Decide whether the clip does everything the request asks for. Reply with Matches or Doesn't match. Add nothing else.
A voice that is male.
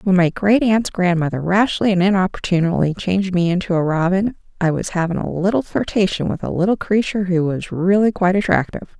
Doesn't match